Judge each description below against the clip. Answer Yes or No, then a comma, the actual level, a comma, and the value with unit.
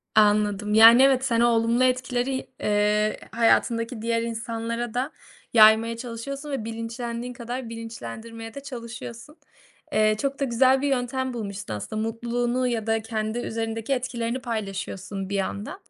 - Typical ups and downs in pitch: No, narrow, 2.1 semitones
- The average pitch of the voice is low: No, high, 230 Hz